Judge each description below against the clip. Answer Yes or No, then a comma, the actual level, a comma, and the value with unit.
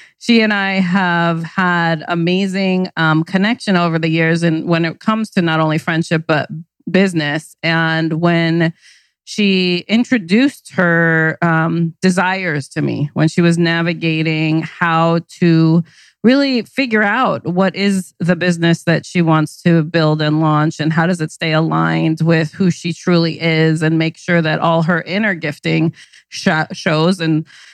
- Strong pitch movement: No, narrow, 2.5 semitones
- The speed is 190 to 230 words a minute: No, average, 155 wpm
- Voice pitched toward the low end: No, medium, 165 Hz